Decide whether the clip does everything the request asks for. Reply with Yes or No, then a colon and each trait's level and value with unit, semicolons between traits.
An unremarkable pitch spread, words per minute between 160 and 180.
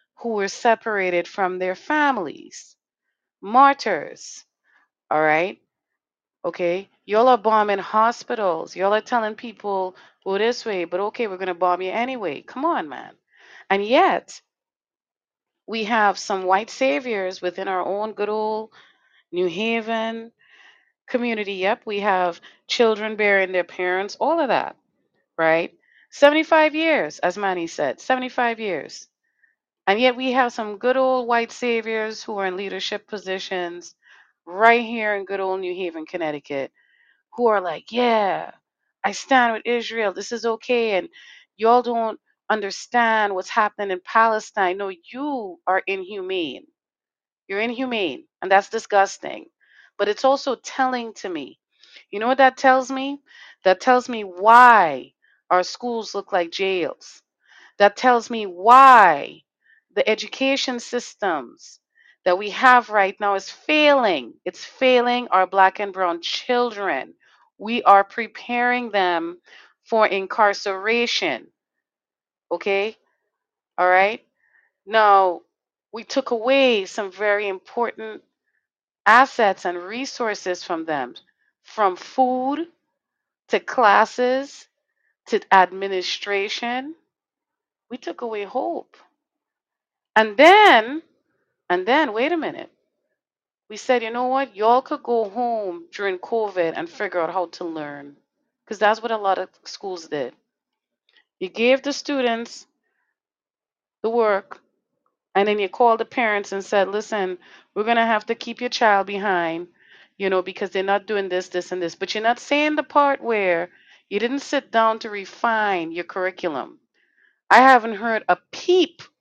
No: average, 4.5 semitones; average, 140 wpm